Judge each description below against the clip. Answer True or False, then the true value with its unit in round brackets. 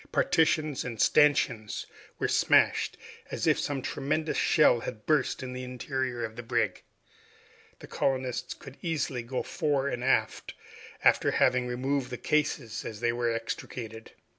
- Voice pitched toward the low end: True (125 Hz)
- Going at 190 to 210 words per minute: False (145 wpm)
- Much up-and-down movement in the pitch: False (3.1 semitones)